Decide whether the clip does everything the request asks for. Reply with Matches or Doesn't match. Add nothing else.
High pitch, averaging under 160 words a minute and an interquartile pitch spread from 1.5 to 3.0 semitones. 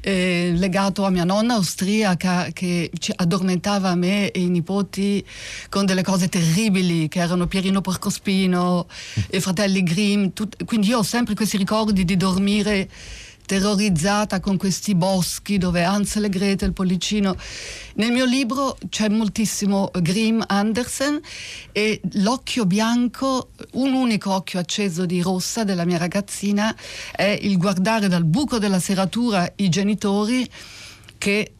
Matches